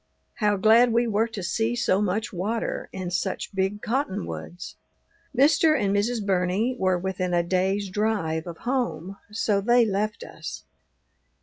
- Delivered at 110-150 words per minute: Yes, average, 145 wpm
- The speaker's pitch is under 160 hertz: No, high, 205 Hz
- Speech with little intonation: No, average, 3.4 semitones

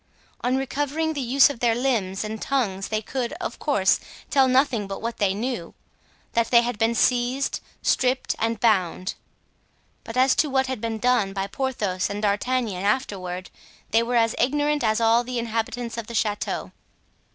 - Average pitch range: Yes, average, 3.5 semitones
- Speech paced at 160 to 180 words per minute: Yes, average, 170 wpm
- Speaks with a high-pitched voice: Yes, high, 235 Hz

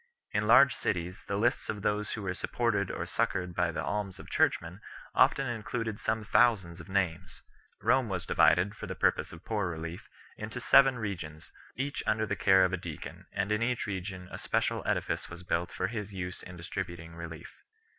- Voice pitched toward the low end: Yes, very low, 95 Hz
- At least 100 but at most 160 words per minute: No, average, 195 wpm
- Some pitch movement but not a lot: Yes, average, 3.6 semitones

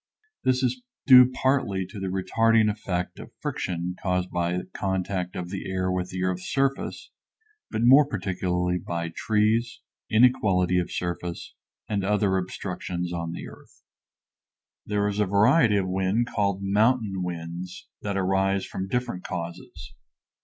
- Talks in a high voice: No, very low, 95 Hz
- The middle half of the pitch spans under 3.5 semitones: Yes, average, 3.0 semitones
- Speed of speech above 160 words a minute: No, average, 140 wpm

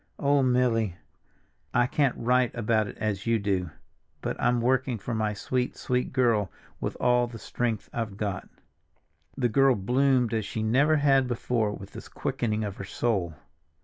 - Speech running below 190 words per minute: Yes, average, 170 wpm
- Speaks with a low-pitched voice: Yes, low, 120 Hz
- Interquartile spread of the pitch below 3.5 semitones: Yes, average, 3.0 semitones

